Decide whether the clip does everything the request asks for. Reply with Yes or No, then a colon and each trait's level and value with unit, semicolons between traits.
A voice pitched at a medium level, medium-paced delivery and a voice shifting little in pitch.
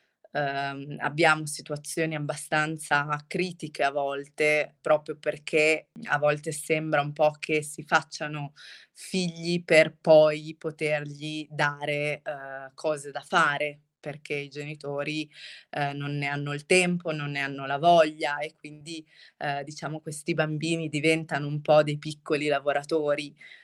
Yes: medium, 150 Hz; average, 130 wpm; narrow, 1.5 semitones